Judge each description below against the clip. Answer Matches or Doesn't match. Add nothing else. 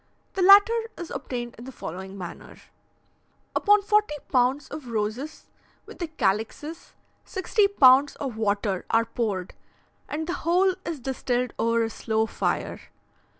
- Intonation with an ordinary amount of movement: Doesn't match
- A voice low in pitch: Doesn't match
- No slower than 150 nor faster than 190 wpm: Doesn't match